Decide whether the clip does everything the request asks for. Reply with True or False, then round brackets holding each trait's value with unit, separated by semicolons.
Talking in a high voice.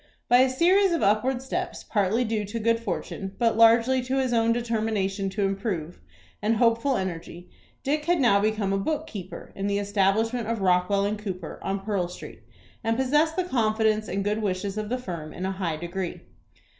True (215 Hz)